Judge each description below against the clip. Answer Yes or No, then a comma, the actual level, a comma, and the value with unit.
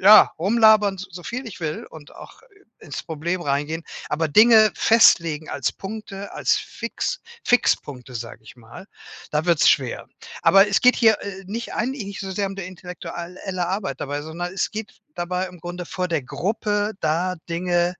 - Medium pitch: Yes, medium, 180 Hz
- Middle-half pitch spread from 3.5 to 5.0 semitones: Yes, average, 4.3 semitones